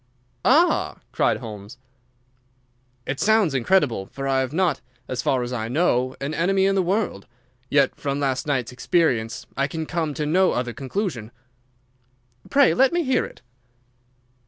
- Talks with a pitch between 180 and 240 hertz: No, medium, 140 Hz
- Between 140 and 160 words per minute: Yes, average, 155 wpm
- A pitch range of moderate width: No, wide, 6.9 semitones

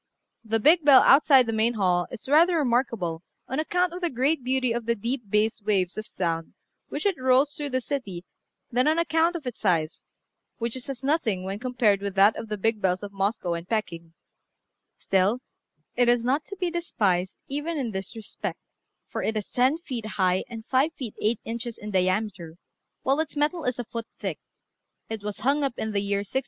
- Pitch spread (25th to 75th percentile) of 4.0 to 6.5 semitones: Yes, wide, 5.4 semitones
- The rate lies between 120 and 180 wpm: No, fast, 205 wpm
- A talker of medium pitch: No, high, 235 Hz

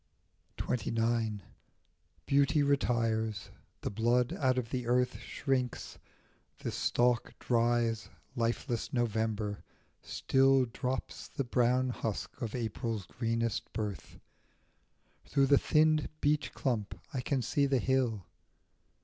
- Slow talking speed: Yes, slow, 105 wpm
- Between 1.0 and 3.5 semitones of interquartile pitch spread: Yes, average, 2.8 semitones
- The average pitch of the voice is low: Yes, low, 120 Hz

